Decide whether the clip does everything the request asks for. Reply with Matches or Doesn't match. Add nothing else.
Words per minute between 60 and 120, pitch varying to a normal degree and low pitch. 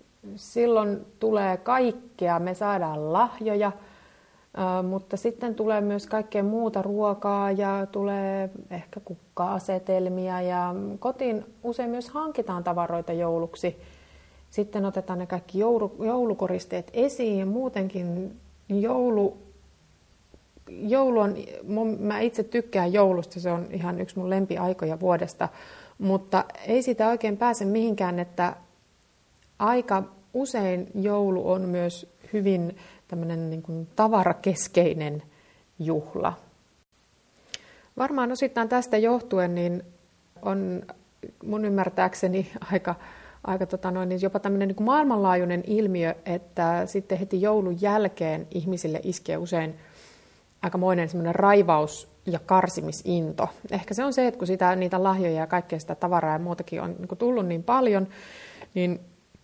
Doesn't match